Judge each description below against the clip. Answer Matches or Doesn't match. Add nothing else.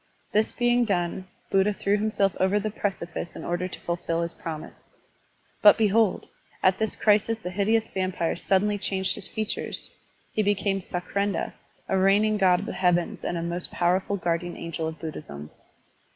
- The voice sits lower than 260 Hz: Matches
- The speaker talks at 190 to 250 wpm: Doesn't match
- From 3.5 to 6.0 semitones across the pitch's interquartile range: Doesn't match